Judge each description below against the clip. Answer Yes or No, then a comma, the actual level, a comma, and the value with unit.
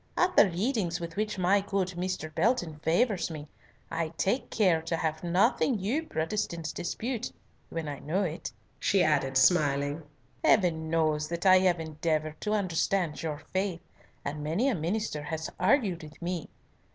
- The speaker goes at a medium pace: Yes, average, 160 wpm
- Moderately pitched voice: Yes, medium, 170 Hz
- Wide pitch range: No, average, 3.9 semitones